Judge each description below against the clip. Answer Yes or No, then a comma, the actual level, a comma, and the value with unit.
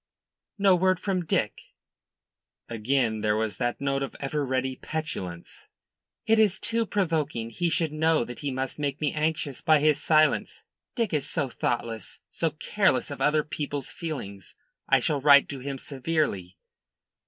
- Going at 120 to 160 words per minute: Yes, average, 155 wpm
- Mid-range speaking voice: Yes, medium, 145 Hz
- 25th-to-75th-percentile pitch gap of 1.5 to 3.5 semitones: No, average, 3.9 semitones